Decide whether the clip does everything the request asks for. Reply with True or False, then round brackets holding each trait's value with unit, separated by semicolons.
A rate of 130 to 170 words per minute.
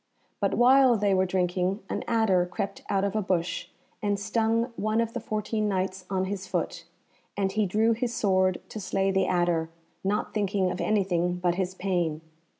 False (180 wpm)